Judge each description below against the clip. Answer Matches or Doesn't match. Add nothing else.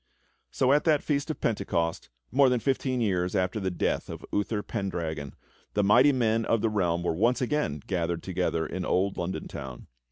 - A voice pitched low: Matches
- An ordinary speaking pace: Matches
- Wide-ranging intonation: Matches